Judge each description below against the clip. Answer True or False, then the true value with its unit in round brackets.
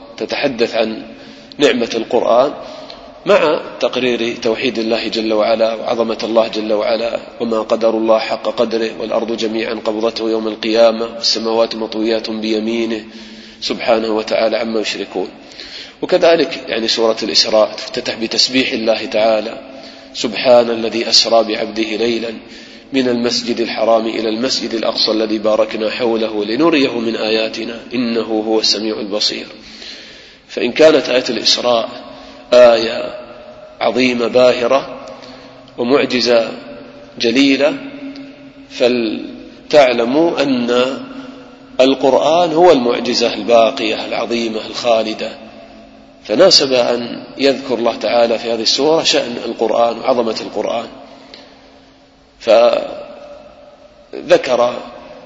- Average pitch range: False (2.2 semitones)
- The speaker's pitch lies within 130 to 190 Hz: False (115 Hz)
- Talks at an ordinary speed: False (100 wpm)